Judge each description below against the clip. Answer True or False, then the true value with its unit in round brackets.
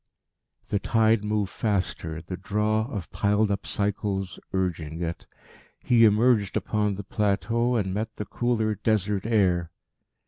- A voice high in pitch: False (105 Hz)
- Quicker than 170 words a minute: False (135 wpm)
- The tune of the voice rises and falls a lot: False (2.4 semitones)